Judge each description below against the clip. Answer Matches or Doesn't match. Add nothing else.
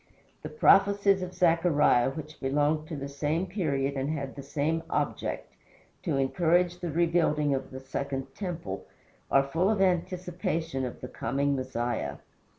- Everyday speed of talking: Matches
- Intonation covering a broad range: Doesn't match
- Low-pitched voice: Doesn't match